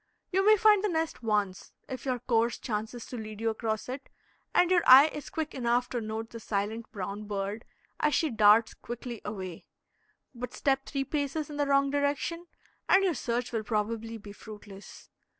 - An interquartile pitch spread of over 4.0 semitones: Yes, average, 4.8 semitones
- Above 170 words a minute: Yes, average, 185 wpm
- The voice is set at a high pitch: Yes, high, 235 Hz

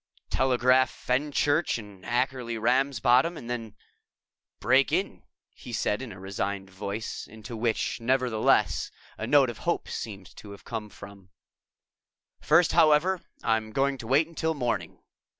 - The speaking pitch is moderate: No, low, 120 Hz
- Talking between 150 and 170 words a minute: No, slow, 135 wpm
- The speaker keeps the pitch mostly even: No, average, 4.1 semitones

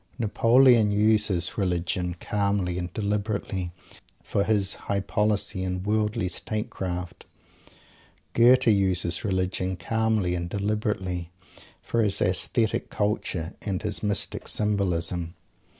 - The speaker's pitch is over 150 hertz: No, low, 100 Hz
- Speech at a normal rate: No, slow, 105 wpm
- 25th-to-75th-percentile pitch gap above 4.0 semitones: No, average, 2.7 semitones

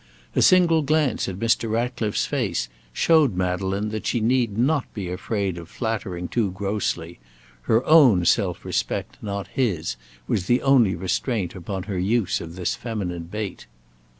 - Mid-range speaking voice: No, low, 105 Hz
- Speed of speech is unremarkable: Yes, average, 150 wpm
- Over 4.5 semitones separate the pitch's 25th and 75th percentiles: Yes, average, 4.9 semitones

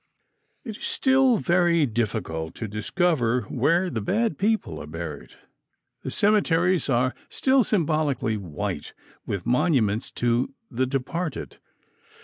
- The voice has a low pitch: No, medium, 145 Hz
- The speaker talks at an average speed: No, slow, 120 wpm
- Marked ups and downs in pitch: Yes, wide, 7.8 semitones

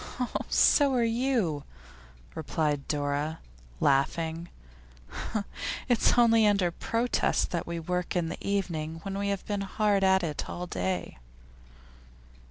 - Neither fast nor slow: No, slow, 120 wpm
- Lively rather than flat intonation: No, average, 4.7 semitones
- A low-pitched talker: No, medium, 180 Hz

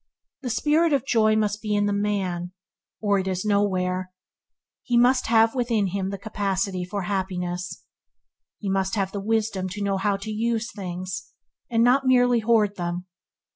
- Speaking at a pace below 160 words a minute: No, average, 175 wpm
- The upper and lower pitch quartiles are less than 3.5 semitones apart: Yes, average, 3.1 semitones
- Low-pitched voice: No, high, 205 Hz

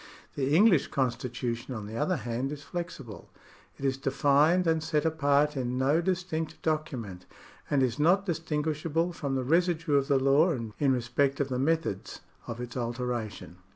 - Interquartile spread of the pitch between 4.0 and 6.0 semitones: Yes, average, 4.4 semitones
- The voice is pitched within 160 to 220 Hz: No, medium, 140 Hz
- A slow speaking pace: No, average, 160 wpm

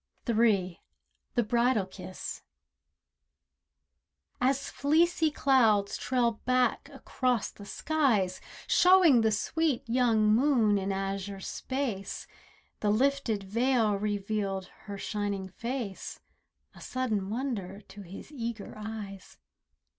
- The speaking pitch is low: No, high, 220 Hz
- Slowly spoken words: Yes, slow, 100 wpm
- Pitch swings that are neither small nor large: Yes, average, 4.5 semitones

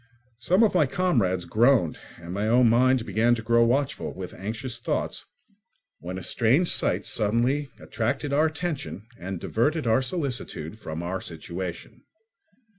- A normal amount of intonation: No, wide, 6.5 semitones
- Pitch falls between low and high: No, low, 115 Hz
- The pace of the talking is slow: No, average, 150 wpm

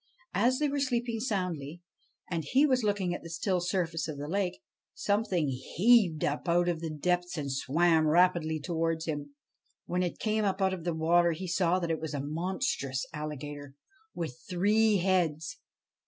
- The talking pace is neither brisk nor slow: Yes, average, 175 wpm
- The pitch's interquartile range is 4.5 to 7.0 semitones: No, average, 3.4 semitones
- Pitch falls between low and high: Yes, medium, 175 Hz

